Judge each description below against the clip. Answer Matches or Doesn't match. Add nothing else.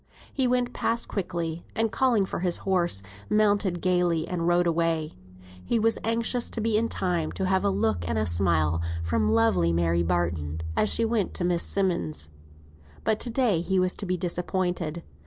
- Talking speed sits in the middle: Matches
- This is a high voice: Doesn't match